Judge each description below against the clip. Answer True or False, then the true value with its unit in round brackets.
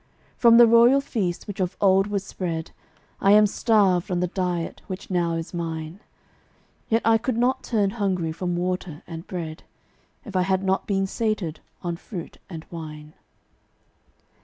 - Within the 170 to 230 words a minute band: False (160 wpm)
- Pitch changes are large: False (3.5 semitones)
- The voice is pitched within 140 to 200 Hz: True (185 Hz)